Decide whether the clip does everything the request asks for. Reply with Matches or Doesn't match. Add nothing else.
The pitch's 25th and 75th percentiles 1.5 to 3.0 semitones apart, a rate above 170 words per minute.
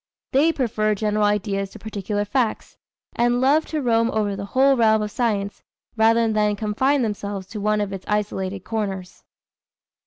Doesn't match